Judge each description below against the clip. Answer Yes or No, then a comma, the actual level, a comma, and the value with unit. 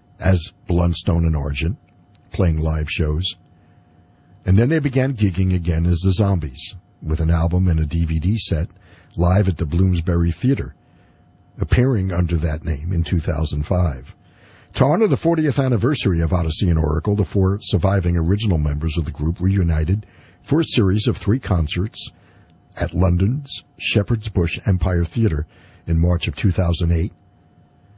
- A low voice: Yes, very low, 90 Hz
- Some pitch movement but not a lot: Yes, average, 3.4 semitones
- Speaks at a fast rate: No, average, 145 wpm